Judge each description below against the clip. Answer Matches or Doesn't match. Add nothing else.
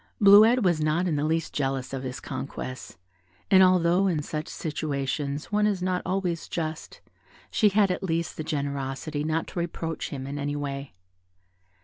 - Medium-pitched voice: Matches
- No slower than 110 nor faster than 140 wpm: Doesn't match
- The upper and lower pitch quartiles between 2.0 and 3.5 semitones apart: Doesn't match